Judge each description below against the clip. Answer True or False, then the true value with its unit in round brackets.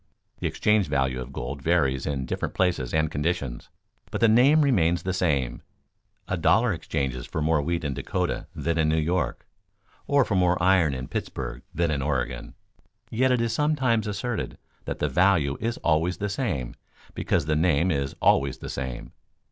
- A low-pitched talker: True (80 Hz)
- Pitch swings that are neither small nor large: False (6.2 semitones)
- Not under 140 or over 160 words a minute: False (175 wpm)